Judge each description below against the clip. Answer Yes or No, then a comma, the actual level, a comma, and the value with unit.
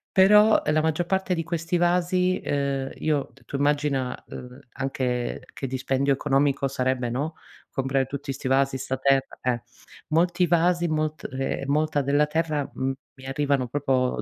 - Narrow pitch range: No, average, 3.2 semitones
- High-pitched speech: No, medium, 140 Hz